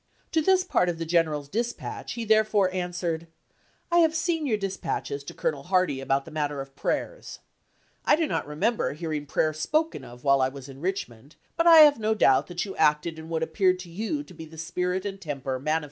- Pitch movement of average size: No, wide, 6.5 semitones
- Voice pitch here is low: No, medium, 170 Hz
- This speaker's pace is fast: Yes, fast, 220 wpm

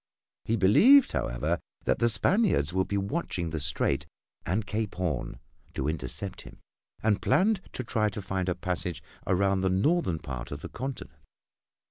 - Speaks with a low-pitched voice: Yes, very low, 95 Hz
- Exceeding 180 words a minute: No, average, 160 wpm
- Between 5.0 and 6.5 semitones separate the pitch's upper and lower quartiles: Yes, wide, 5.6 semitones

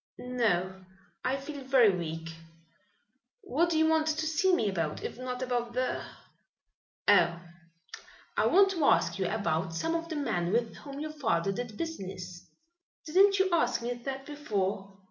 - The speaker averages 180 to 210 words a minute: No, average, 165 wpm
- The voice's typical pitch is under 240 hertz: No, very high, 250 Hz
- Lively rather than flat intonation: Yes, wide, 8.1 semitones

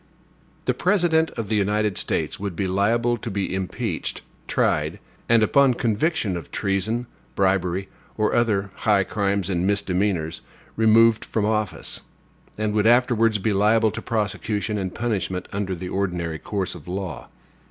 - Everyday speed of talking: Yes, average, 145 wpm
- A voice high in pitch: No, low, 105 Hz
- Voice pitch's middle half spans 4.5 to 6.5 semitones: No, average, 2.9 semitones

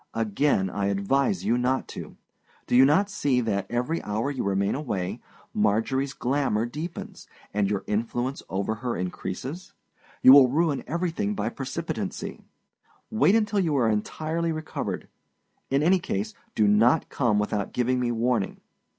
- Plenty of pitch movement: Yes, wide, 6.3 semitones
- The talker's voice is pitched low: Yes, low, 125 Hz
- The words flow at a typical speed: Yes, average, 150 wpm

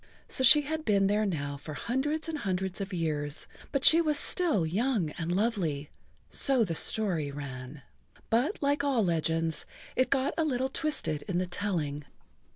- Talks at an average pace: Yes, average, 160 wpm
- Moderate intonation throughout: No, wide, 9.0 semitones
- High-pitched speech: Yes, high, 200 Hz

